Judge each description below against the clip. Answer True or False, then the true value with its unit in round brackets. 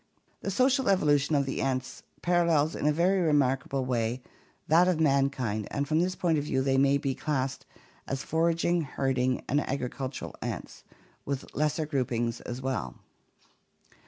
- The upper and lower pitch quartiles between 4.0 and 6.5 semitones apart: False (3.6 semitones)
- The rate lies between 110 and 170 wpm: True (155 wpm)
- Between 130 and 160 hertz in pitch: True (140 Hz)